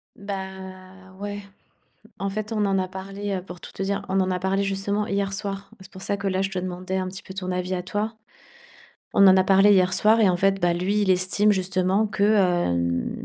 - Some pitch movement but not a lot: No, narrow, 1.4 semitones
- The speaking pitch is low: No, high, 190 Hz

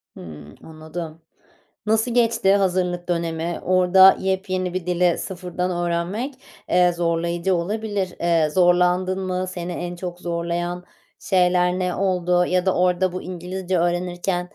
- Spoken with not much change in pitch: Yes, narrow, 1.3 semitones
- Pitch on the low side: No, medium, 180 Hz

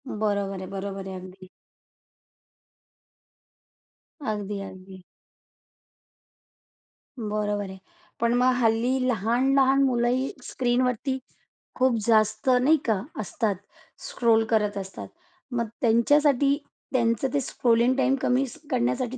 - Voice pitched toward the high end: Yes, high, 230 Hz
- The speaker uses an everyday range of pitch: Yes, average, 3.9 semitones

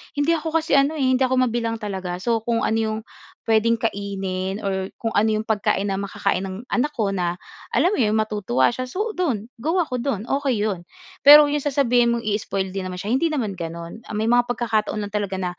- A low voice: No, high, 220 Hz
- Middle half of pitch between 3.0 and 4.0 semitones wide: No, average, 4.7 semitones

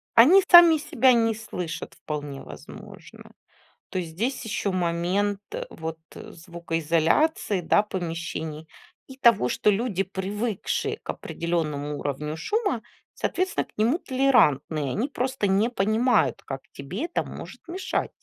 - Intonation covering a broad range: Yes, wide, 7.0 semitones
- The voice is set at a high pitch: Yes, high, 195 Hz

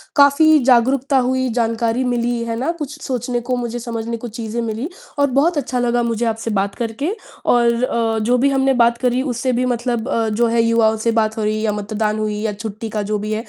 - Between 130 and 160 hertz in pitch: No, high, 235 Hz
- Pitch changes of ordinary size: No, narrow, 2.3 semitones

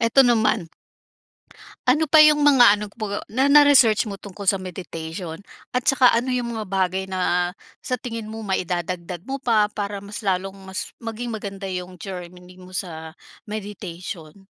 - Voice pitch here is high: Yes, high, 200 Hz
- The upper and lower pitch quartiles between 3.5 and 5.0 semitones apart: Yes, average, 4.4 semitones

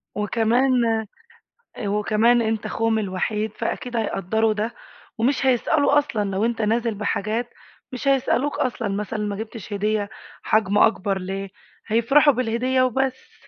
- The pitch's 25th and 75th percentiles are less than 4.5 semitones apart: Yes, average, 2.9 semitones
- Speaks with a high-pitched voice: Yes, high, 225 Hz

